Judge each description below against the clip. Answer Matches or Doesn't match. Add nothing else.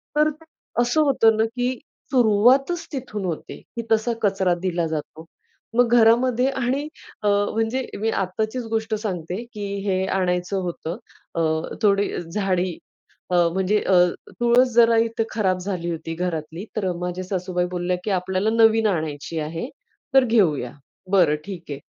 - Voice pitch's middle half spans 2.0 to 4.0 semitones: Doesn't match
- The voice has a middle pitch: Doesn't match